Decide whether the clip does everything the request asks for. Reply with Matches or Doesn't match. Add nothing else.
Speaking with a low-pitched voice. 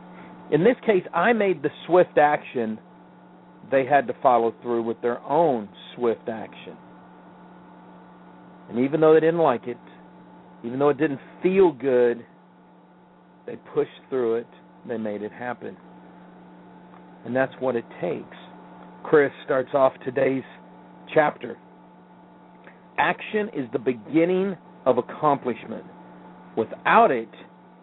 Matches